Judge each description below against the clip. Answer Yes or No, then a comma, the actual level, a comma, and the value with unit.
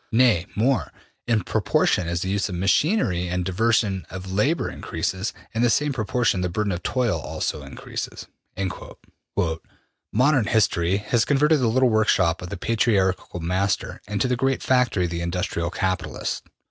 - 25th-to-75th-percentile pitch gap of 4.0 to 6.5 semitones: Yes, average, 5.1 semitones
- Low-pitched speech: Yes, low, 100 Hz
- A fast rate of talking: No, average, 155 wpm